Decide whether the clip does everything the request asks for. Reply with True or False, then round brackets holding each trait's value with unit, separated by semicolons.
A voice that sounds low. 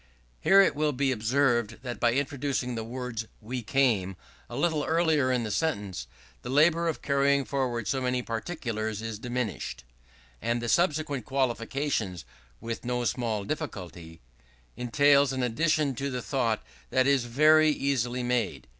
True (125 Hz)